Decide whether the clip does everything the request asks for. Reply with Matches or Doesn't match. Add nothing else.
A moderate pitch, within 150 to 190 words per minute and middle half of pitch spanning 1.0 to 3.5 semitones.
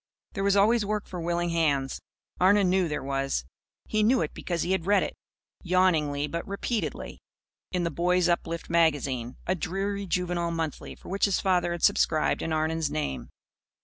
Matches